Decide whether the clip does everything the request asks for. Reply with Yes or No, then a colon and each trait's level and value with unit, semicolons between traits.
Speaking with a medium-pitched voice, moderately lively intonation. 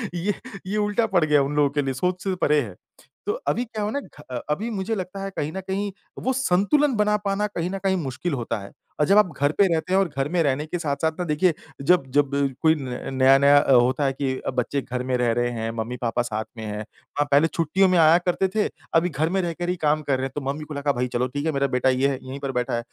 No: medium, 150 Hz; wide, 5.9 semitones